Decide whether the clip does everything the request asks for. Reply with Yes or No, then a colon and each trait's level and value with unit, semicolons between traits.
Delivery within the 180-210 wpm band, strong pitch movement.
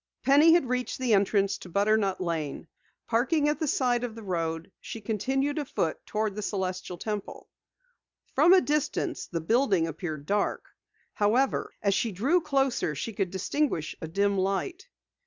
No: average, 155 wpm; wide, 6.3 semitones